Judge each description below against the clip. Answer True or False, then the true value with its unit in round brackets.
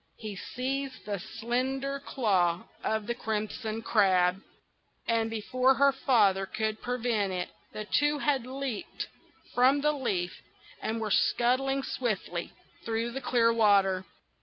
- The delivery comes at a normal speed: False (130 wpm)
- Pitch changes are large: False (4.1 semitones)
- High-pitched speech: True (230 Hz)